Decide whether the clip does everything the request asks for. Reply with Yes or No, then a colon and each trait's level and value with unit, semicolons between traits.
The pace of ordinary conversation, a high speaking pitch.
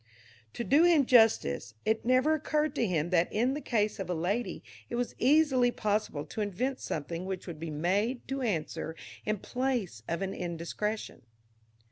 Yes: average, 170 wpm; high, 215 Hz